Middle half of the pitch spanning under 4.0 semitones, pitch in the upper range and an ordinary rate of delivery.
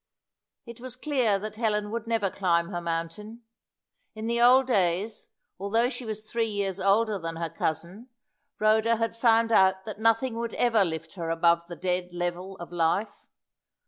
No: average, 4.5 semitones; high, 210 Hz; average, 170 wpm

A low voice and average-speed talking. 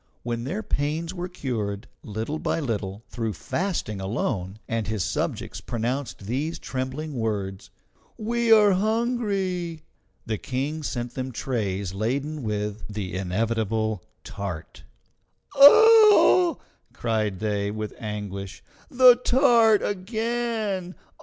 No: low, 125 Hz; slow, 110 wpm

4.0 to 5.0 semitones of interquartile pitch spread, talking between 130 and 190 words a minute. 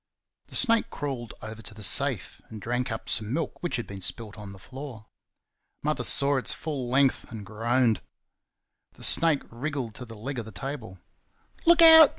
Yes: average, 4.3 semitones; average, 180 wpm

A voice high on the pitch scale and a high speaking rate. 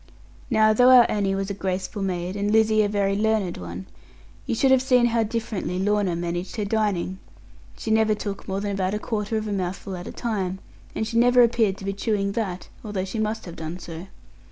Yes: high, 205 Hz; fast, 215 wpm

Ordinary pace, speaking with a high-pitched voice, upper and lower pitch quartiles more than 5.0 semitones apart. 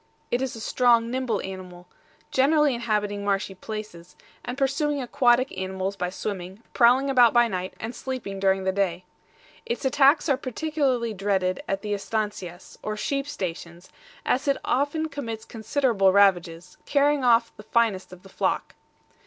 Yes: average, 155 wpm; high, 220 Hz; wide, 5.4 semitones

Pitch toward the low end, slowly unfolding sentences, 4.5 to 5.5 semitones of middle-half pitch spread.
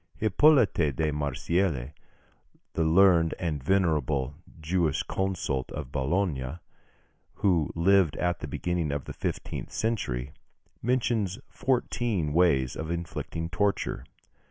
Yes: very low, 85 Hz; slow, 105 wpm; average, 4.8 semitones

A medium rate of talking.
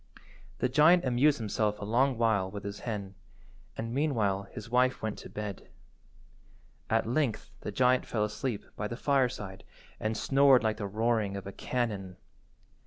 Yes: average, 160 wpm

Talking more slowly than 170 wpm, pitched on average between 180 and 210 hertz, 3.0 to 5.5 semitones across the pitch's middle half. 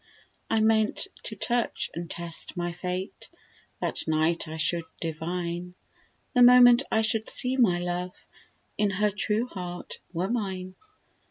Yes: average, 140 wpm; medium, 185 Hz; average, 4.2 semitones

